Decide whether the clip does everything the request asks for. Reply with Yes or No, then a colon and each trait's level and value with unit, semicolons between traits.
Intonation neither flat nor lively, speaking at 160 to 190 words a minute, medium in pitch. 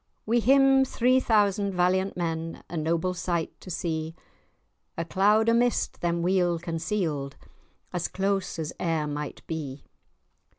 No: average, 4.0 semitones; slow, 135 wpm; medium, 175 Hz